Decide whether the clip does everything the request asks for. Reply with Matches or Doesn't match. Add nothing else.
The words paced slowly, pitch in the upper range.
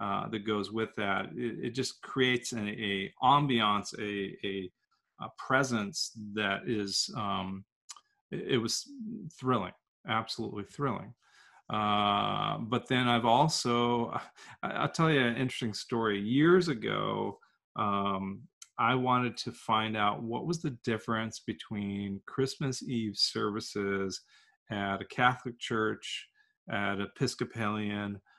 Doesn't match